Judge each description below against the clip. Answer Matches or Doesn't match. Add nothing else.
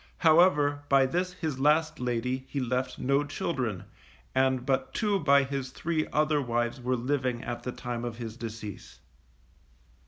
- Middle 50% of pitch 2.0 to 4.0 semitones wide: Matches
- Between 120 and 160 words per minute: Matches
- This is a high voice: Doesn't match